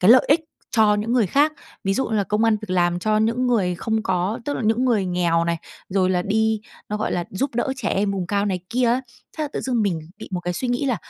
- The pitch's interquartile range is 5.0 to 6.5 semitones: No, average, 4.5 semitones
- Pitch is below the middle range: No, high, 215 Hz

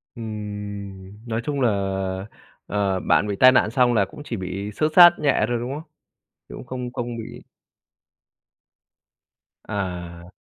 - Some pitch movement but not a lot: Yes, average, 4.0 semitones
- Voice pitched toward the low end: Yes, low, 110 Hz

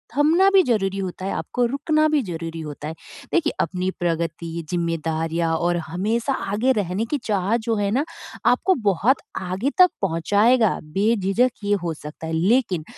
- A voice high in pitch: Yes, high, 195 Hz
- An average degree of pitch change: No, wide, 6.7 semitones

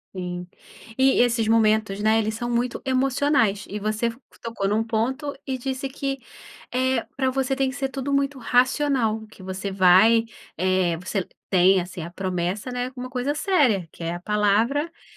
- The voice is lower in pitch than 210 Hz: No, high, 230 Hz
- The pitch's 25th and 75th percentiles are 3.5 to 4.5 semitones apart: No, average, 5.0 semitones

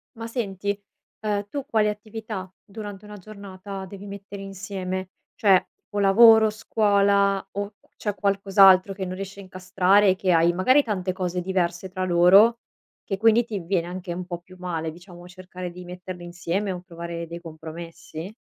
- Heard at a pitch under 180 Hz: No, high, 190 Hz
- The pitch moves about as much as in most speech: No, narrow, 2.2 semitones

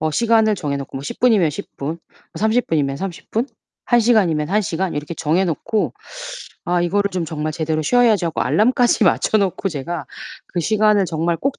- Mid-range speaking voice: Yes, medium, 180 Hz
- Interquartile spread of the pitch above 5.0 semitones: Yes, wide, 5.6 semitones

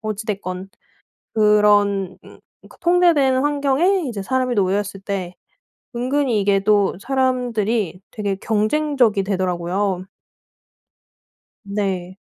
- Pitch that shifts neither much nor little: Yes, average, 4.8 semitones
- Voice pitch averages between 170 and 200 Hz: No, high, 210 Hz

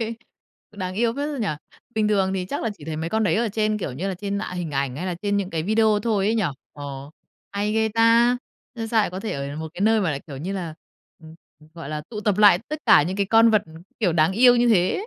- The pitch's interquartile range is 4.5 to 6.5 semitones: Yes, average, 5.1 semitones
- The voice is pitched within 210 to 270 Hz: No, high, 200 Hz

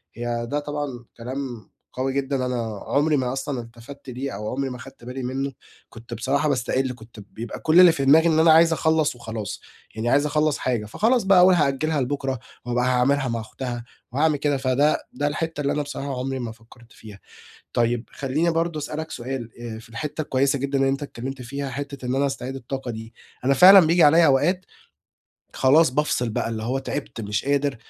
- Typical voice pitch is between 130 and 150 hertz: Yes, low, 135 Hz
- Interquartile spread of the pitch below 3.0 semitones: No, average, 3.3 semitones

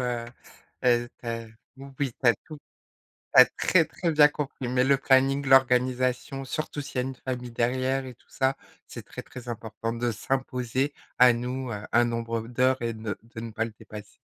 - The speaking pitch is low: Yes, low, 125 Hz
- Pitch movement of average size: No, narrow, 2.2 semitones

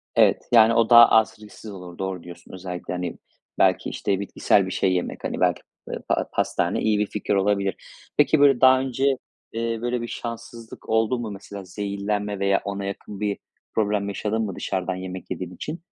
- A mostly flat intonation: No, average, 3.0 semitones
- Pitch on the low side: Yes, low, 105 Hz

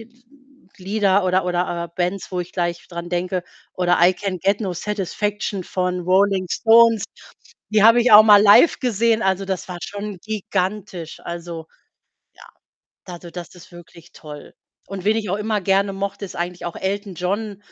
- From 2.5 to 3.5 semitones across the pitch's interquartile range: Yes, average, 2.8 semitones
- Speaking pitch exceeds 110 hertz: Yes, high, 190 Hz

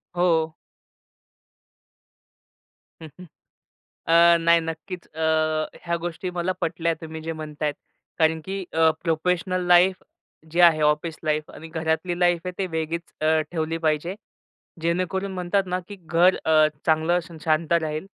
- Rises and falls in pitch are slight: Yes, narrow, 2.0 semitones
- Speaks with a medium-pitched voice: Yes, medium, 165 Hz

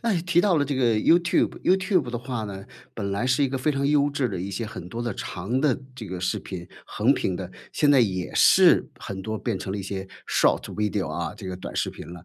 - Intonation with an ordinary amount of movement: No, wide, 6.7 semitones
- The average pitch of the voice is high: No, low, 115 Hz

